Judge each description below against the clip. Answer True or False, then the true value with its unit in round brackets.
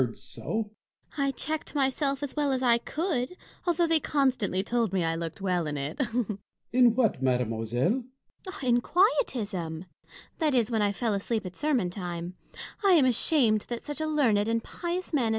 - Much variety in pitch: True (7.2 semitones)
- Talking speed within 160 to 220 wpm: True (180 wpm)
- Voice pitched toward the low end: False (240 Hz)